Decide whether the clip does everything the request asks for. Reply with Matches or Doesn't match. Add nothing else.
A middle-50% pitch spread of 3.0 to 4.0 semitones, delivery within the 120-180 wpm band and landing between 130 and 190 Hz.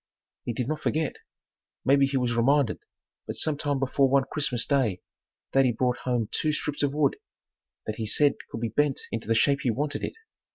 Doesn't match